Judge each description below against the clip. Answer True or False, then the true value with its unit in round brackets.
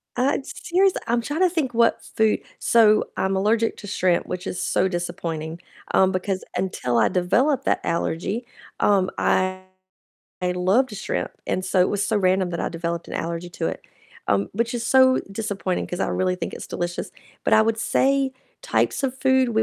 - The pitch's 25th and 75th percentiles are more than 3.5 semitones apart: True (5.0 semitones)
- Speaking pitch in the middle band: False (195 Hz)